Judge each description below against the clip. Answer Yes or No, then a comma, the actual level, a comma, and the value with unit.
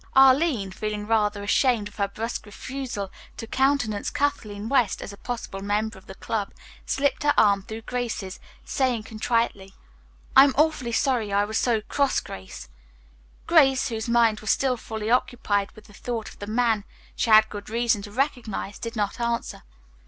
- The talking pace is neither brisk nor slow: Yes, average, 170 wpm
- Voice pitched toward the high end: Yes, high, 220 Hz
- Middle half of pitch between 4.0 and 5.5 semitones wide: No, average, 3.3 semitones